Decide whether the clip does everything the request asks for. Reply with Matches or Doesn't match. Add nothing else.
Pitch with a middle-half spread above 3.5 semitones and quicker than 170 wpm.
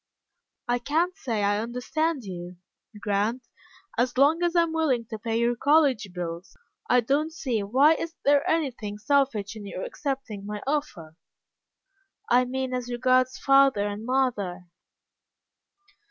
Doesn't match